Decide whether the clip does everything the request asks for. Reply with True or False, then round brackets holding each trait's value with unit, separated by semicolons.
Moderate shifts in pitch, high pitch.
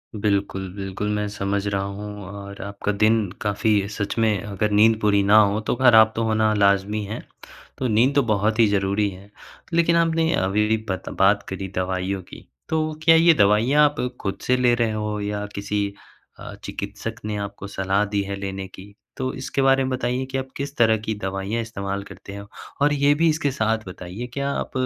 False (3.1 semitones; 105 Hz)